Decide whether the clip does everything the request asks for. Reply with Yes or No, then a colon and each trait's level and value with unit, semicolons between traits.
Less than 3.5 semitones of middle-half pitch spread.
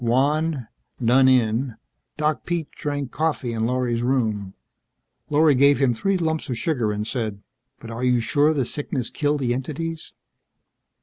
No: average, 4.2 semitones